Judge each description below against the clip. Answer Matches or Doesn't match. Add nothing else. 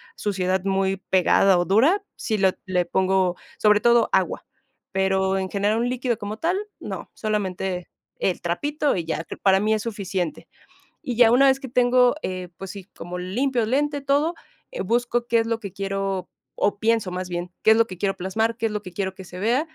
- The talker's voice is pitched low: Doesn't match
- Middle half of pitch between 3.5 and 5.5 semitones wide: Matches